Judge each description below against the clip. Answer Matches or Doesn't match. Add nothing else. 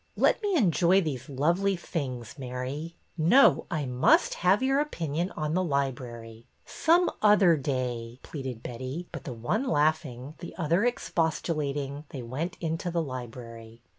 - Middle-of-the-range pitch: Matches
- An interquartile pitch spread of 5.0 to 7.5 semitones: Matches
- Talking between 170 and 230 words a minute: Doesn't match